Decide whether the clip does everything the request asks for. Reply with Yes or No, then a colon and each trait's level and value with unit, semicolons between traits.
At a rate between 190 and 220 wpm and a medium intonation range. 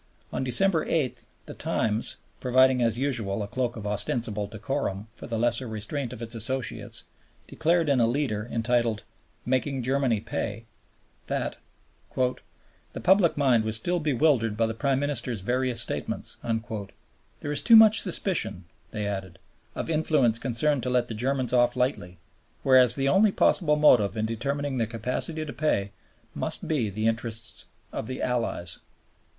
No: average, 155 wpm; average, 4.0 semitones